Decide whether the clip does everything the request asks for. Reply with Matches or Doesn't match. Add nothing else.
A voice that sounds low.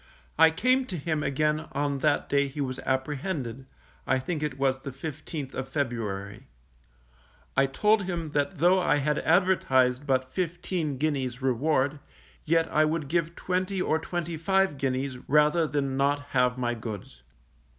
Doesn't match